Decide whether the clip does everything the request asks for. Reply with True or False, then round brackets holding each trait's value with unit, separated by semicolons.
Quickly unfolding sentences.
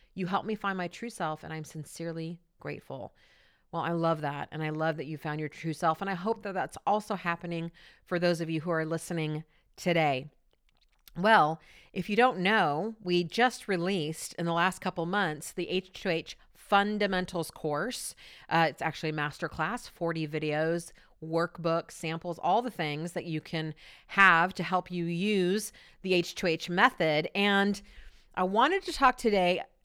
False (170 wpm)